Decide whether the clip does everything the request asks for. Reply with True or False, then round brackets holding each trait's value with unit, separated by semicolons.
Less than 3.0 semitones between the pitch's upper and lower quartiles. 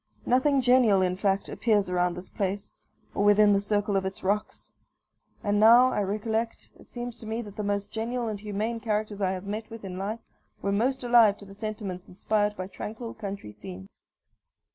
True (2.4 semitones)